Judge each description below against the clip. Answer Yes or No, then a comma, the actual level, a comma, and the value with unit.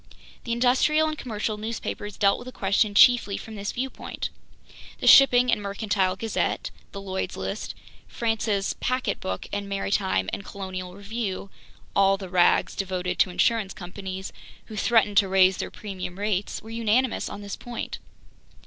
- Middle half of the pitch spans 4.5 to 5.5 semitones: No, average, 3.1 semitones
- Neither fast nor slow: Yes, average, 145 wpm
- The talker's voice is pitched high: Yes, high, 200 Hz